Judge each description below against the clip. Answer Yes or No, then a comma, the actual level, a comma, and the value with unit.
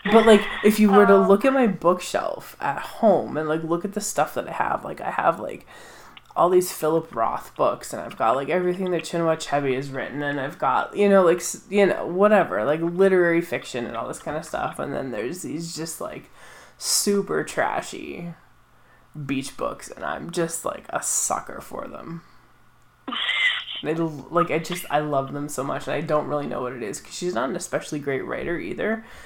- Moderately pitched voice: Yes, medium, 170 Hz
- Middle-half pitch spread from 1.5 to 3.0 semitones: No, average, 4.8 semitones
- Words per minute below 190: No, fast, 205 wpm